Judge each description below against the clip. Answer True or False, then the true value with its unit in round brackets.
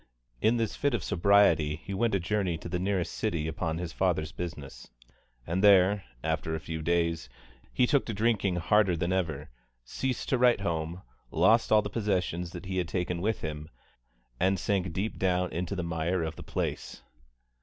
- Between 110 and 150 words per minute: False (185 wpm)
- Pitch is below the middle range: True (90 Hz)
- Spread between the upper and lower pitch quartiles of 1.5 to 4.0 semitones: True (3.7 semitones)